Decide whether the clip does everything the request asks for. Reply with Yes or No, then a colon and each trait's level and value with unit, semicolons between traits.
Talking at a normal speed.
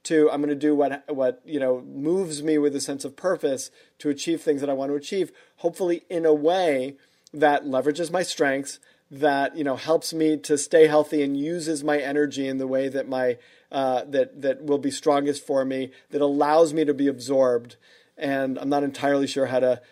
No: fast, 210 wpm